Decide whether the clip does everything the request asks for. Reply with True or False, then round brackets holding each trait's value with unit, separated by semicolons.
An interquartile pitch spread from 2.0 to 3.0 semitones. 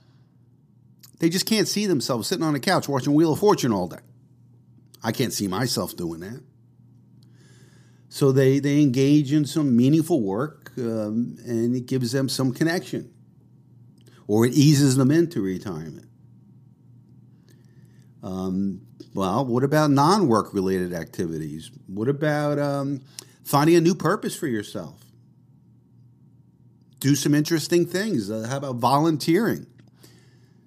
False (4.2 semitones)